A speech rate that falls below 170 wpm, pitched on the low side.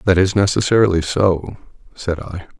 Yes: average, 140 wpm; very low, 95 Hz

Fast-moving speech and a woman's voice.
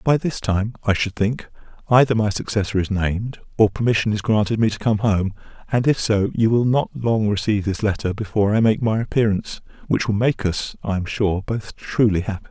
No: fast, 210 wpm; male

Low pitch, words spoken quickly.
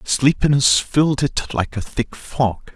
No: low, 130 Hz; average, 155 wpm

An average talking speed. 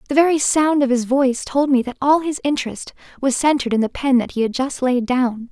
No: fast, 250 wpm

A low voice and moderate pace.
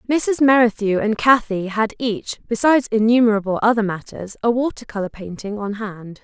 No: high, 220 Hz; average, 155 wpm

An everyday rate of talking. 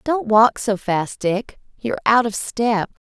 Yes: average, 175 wpm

